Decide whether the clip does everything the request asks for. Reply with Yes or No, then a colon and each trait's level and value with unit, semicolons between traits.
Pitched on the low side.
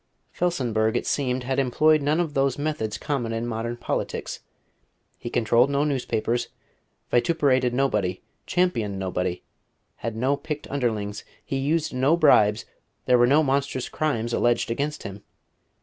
Yes: low, 125 Hz